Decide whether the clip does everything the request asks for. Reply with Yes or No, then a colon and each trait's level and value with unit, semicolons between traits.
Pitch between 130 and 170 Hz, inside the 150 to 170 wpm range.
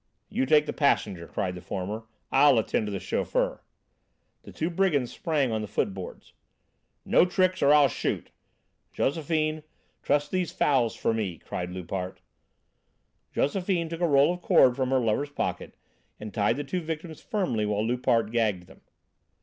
Yes: low, 135 Hz; average, 160 wpm